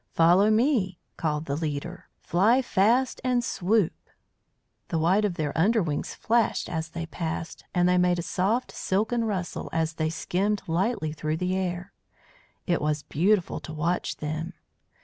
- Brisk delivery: No, average, 155 wpm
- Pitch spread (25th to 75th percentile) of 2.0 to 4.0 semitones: No, average, 4.4 semitones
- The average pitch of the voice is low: No, medium, 180 Hz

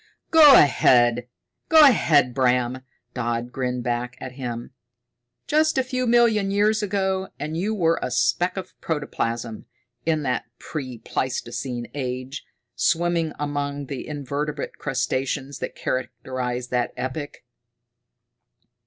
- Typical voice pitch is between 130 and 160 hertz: Yes, medium, 140 Hz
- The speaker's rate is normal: No, slow, 120 wpm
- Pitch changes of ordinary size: No, wide, 5.7 semitones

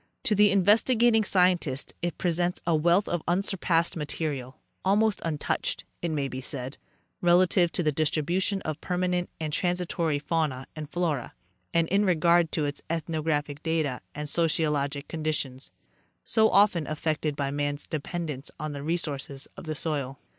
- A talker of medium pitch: Yes, medium, 160 Hz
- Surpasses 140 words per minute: Yes, average, 150 wpm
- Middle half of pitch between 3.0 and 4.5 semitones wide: Yes, average, 3.3 semitones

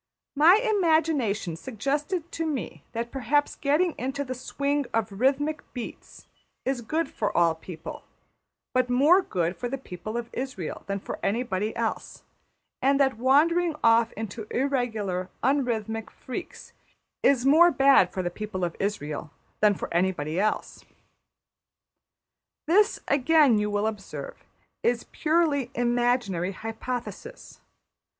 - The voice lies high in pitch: Yes, high, 245 Hz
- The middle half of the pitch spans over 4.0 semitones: Yes, wide, 5.5 semitones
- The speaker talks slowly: Yes, slow, 130 wpm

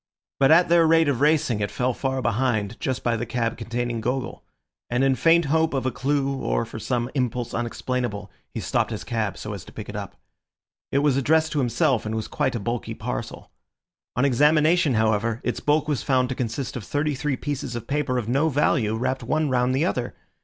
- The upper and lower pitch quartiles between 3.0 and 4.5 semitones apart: Yes, average, 3.8 semitones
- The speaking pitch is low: Yes, low, 130 Hz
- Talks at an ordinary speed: No, fast, 210 wpm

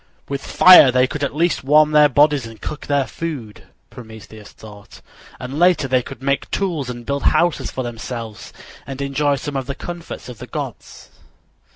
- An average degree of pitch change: Yes, average, 3.4 semitones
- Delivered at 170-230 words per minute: Yes, average, 180 wpm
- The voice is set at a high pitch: No, medium, 140 Hz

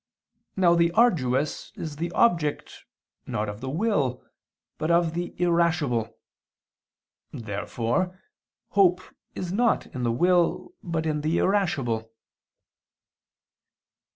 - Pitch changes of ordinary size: No, wide, 5.8 semitones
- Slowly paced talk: Yes, slow, 105 wpm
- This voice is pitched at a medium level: Yes, medium, 165 Hz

